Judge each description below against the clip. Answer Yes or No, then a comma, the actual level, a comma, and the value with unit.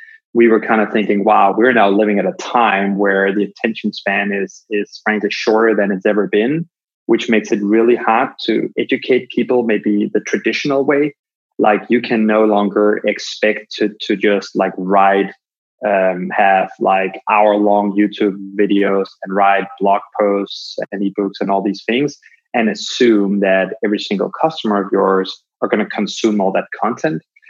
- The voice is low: Yes, low, 105 Hz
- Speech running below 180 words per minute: Yes, average, 170 wpm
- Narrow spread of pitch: Yes, narrow, 1.8 semitones